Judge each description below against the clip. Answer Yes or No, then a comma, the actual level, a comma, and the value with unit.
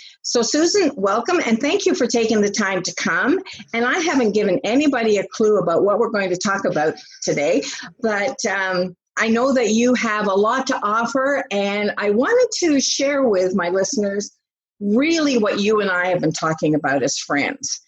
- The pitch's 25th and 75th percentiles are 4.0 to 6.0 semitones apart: Yes, average, 5.2 semitones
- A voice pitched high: Yes, high, 220 Hz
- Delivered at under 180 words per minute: No, average, 190 wpm